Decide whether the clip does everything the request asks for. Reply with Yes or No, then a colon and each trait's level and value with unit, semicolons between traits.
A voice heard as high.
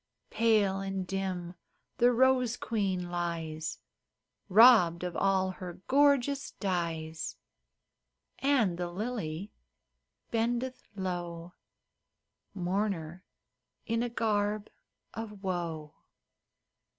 Yes: high, 195 Hz